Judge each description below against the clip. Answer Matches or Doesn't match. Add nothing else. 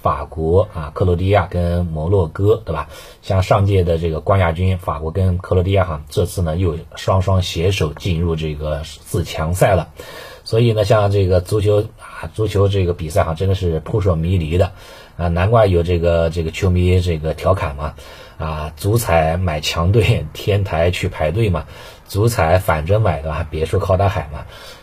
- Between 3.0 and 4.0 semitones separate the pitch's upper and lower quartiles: Matches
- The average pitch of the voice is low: Matches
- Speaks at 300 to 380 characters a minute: Doesn't match